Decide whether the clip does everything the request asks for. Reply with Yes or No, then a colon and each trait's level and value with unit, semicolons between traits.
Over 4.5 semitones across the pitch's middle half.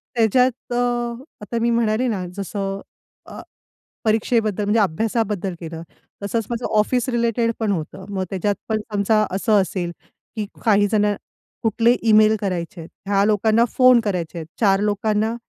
No: average, 2.9 semitones